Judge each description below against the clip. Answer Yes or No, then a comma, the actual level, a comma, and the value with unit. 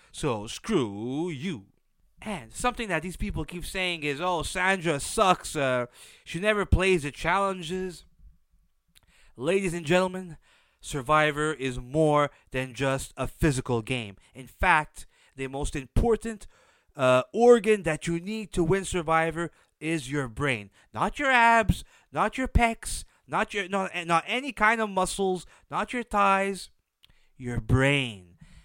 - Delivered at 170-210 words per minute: No, average, 140 wpm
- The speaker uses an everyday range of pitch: No, wide, 6.4 semitones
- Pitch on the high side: No, medium, 165 Hz